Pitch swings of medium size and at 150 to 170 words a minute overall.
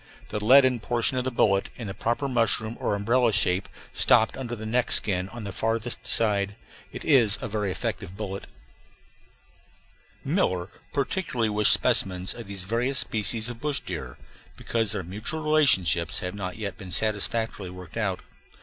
Yes: average, 3.5 semitones; average, 160 wpm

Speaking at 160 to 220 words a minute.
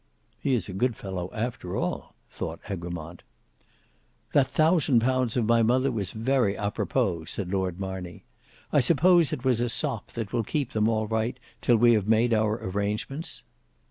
Yes: average, 175 wpm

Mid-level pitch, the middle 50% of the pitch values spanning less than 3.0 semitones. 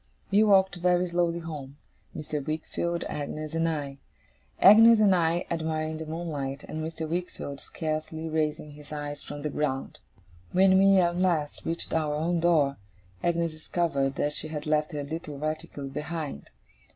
Yes: medium, 155 Hz; narrow, 2.5 semitones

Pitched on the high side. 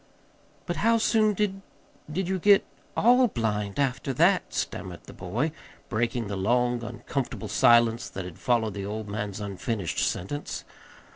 No: low, 120 Hz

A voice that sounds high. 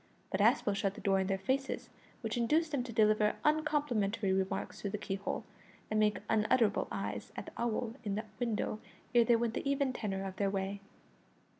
Yes: high, 215 Hz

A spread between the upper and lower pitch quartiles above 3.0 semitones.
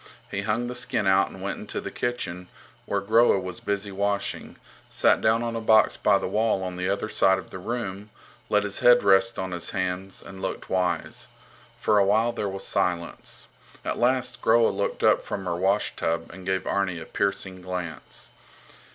No: average, 2.7 semitones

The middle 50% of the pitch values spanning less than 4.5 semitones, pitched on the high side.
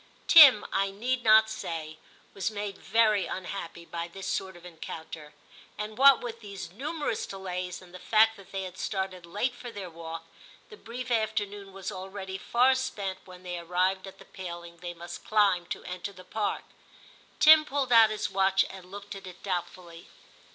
Yes: average, 3.3 semitones; high, 195 Hz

